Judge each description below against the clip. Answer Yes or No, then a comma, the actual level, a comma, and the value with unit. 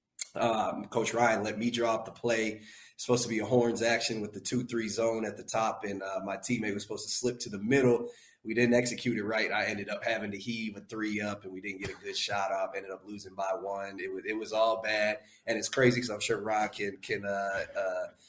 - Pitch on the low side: Yes, low, 110 Hz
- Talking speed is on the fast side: Yes, fast, 255 wpm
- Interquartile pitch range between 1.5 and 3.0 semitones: Yes, average, 2.7 semitones